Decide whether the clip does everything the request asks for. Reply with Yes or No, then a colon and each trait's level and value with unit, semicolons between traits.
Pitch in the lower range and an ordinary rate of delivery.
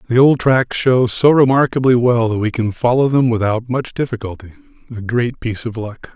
Yes: low, 120 Hz; average, 185 wpm